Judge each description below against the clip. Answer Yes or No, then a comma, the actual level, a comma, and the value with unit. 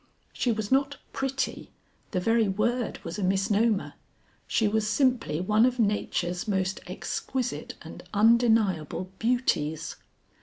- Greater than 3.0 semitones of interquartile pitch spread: Yes, average, 4.2 semitones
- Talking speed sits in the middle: No, slow, 120 wpm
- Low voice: No, high, 215 Hz